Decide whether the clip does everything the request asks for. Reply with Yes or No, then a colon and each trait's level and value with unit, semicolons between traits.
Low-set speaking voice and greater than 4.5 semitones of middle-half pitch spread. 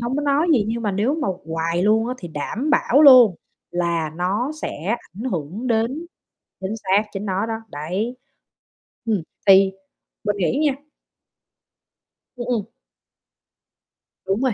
No: high, 215 Hz; average, 4.9 semitones